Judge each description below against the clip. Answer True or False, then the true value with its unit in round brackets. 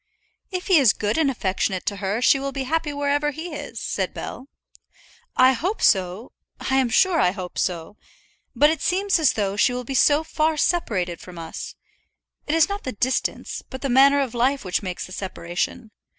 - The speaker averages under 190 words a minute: False (195 wpm)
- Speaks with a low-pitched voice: False (260 Hz)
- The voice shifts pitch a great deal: True (6.9 semitones)